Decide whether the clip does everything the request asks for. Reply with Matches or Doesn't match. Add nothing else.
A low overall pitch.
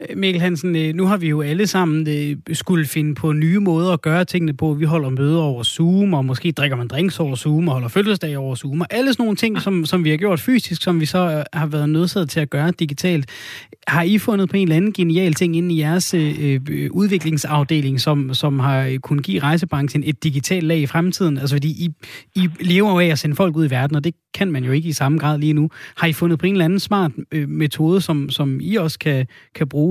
Doesn't match